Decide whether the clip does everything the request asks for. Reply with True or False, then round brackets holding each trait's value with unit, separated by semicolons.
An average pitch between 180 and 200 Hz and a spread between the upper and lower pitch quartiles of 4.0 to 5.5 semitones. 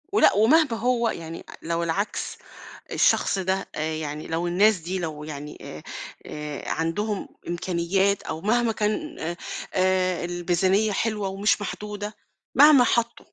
True (190 Hz; 4.3 semitones)